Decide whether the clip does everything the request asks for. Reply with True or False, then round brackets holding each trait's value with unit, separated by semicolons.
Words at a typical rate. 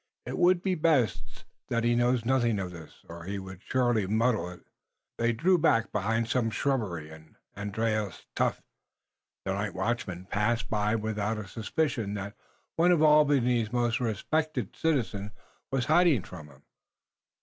True (150 wpm)